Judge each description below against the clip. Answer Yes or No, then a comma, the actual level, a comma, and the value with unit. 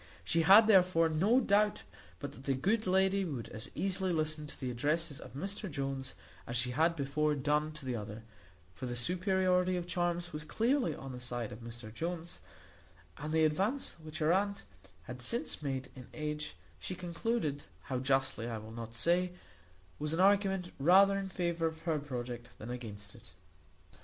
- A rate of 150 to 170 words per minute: No, average, 180 wpm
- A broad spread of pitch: Yes, wide, 5.8 semitones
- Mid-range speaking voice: Yes, medium, 155 Hz